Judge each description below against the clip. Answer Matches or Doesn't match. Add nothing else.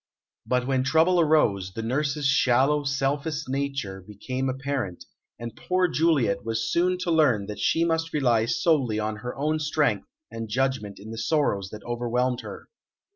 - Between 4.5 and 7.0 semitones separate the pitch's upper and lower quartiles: Matches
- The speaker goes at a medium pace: Matches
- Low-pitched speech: Matches